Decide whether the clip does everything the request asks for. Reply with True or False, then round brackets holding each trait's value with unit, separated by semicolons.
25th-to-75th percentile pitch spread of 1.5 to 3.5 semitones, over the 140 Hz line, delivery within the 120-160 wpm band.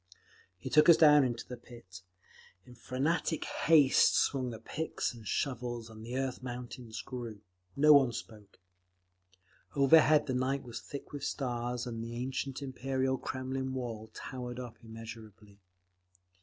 False (2.7 semitones; 125 Hz; 140 wpm)